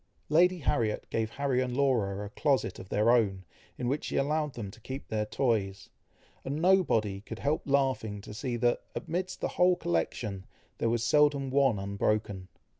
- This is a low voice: Yes, low, 120 Hz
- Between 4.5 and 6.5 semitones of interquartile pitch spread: Yes, average, 5.3 semitones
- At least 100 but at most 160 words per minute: No, average, 175 wpm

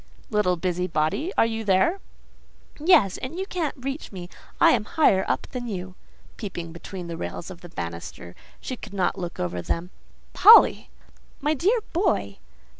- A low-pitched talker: No, high, 195 Hz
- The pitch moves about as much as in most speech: No, wide, 9.0 semitones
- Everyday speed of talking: Yes, average, 155 wpm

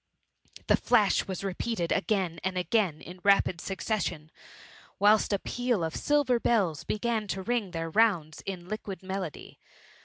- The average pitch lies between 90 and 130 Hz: No, high, 195 Hz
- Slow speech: No, average, 145 wpm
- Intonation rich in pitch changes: No, average, 3.8 semitones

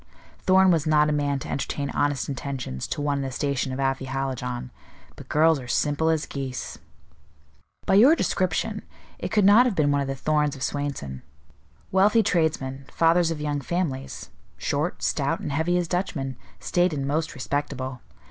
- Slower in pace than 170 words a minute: No, average, 175 wpm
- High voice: No, medium, 145 Hz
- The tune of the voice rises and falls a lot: No, average, 3.4 semitones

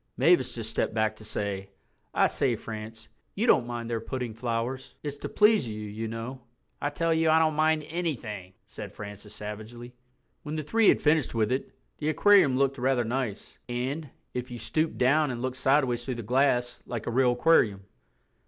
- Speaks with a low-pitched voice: Yes, low, 125 Hz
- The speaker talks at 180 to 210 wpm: Yes, average, 190 wpm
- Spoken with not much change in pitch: No, average, 4.5 semitones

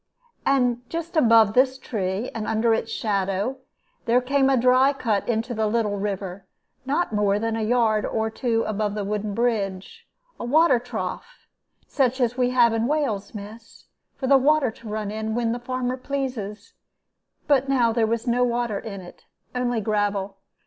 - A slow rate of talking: No, average, 170 wpm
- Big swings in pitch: No, average, 3.2 semitones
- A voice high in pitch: Yes, high, 230 Hz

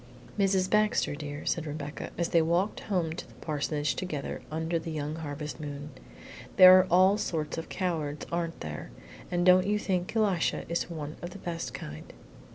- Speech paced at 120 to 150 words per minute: No, average, 175 wpm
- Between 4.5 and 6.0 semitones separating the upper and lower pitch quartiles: No, average, 3.6 semitones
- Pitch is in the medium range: Yes, medium, 165 Hz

